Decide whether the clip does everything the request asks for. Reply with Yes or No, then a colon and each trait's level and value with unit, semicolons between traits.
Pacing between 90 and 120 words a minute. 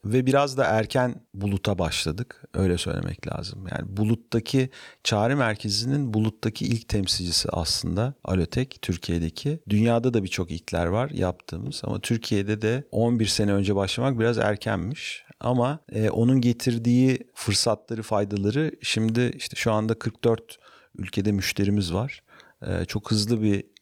No: average, 130 wpm